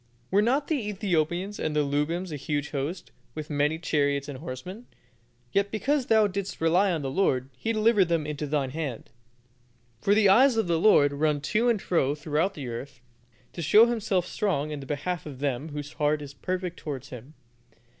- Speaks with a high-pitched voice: No, medium, 160 Hz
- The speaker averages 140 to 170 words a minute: No, average, 195 wpm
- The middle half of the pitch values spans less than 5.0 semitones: No, wide, 5.6 semitones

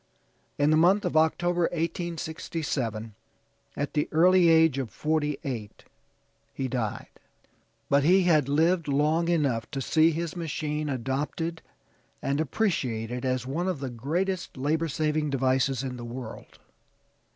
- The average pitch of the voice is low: No, medium, 150 Hz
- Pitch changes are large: No, average, 4.0 semitones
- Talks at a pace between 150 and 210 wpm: No, slow, 135 wpm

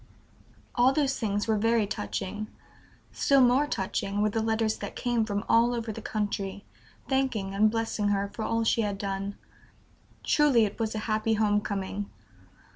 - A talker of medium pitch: No, high, 215 Hz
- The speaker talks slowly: No, average, 165 wpm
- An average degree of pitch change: No, narrow, 2.1 semitones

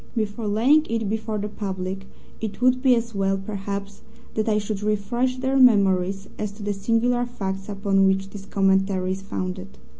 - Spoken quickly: No, average, 175 wpm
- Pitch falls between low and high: No, high, 205 Hz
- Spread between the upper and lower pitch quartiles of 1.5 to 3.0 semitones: Yes, average, 2.7 semitones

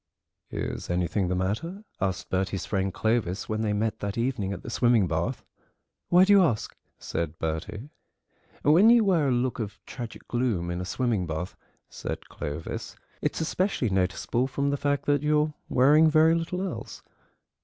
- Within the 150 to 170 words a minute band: Yes, average, 165 wpm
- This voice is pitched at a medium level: No, low, 115 Hz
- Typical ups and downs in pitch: No, wide, 8.0 semitones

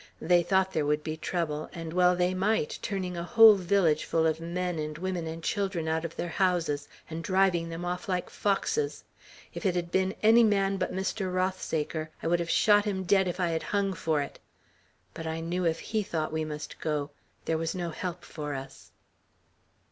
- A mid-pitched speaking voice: Yes, medium, 175 Hz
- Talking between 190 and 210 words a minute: Yes, average, 200 wpm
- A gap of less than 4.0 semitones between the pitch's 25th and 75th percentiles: Yes, average, 2.8 semitones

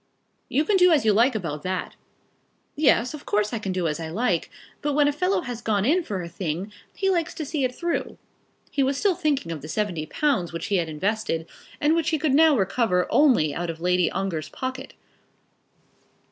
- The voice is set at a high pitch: Yes, high, 225 Hz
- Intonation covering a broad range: Yes, wide, 8.6 semitones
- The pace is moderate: No, fast, 210 wpm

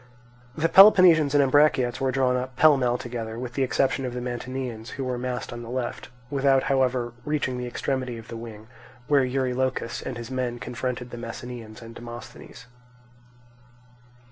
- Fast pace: No, average, 170 wpm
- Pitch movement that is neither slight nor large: No, narrow, 1.9 semitones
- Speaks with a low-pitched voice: Yes, low, 125 Hz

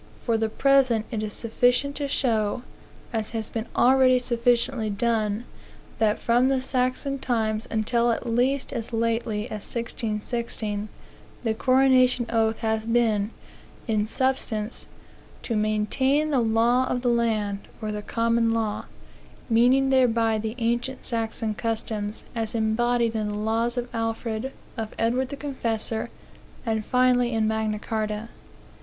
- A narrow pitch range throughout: Yes, narrow, 2.1 semitones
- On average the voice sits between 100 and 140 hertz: No, high, 230 Hz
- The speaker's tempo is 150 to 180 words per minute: No, slow, 135 wpm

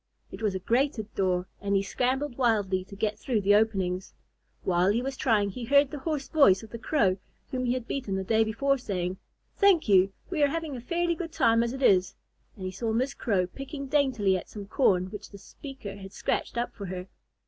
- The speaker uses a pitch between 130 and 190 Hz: No, high, 220 Hz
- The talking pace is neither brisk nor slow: No, fast, 220 wpm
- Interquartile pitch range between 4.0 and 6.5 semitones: Yes, wide, 5.6 semitones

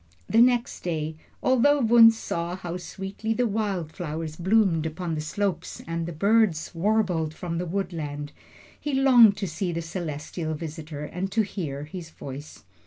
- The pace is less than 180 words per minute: Yes, average, 160 wpm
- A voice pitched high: No, medium, 175 Hz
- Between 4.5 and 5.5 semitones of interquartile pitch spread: Yes, average, 5.0 semitones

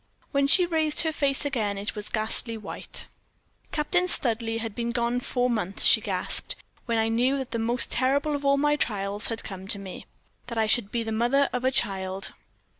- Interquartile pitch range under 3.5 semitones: No, average, 4.2 semitones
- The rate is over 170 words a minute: Yes, average, 200 wpm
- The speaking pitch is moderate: No, high, 235 Hz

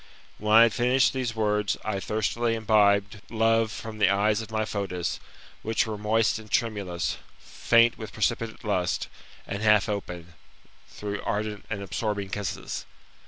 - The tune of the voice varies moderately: No, narrow, 1.8 semitones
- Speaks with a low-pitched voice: Yes, low, 105 Hz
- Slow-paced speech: No, average, 150 wpm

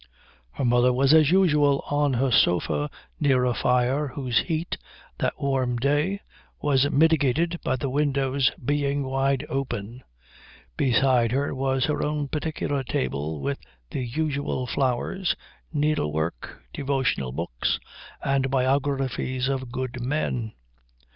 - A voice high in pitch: No, low, 135 Hz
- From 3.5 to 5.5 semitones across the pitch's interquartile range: No, narrow, 2.6 semitones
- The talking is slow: Yes, slow, 120 wpm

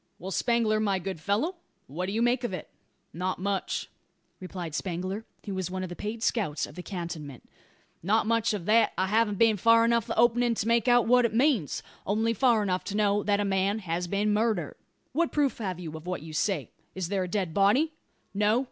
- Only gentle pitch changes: No, average, 3.9 semitones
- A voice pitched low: No, high, 205 Hz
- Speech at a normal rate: No, fast, 220 wpm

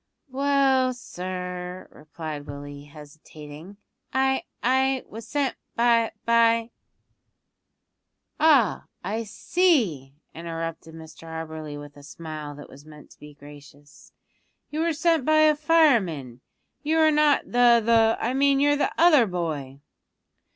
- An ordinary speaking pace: No, slow, 130 wpm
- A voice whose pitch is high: Yes, high, 200 Hz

